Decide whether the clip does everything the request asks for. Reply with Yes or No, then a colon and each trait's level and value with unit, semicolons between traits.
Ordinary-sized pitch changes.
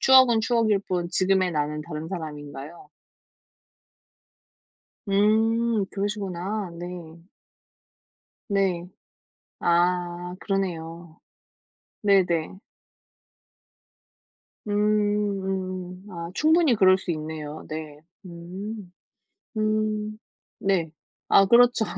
Yes: average, 3.5 semitones